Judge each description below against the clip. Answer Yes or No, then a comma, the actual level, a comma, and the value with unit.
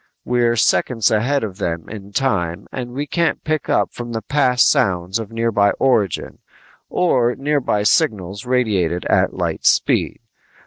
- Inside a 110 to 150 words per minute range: Yes, average, 145 wpm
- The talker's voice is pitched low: Yes, low, 115 Hz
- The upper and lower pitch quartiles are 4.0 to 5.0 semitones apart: Yes, average, 4.3 semitones